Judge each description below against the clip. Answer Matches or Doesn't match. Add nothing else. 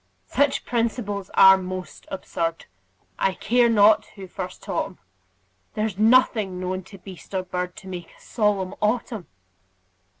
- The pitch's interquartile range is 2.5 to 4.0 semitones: Matches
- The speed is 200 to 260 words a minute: Doesn't match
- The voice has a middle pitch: Doesn't match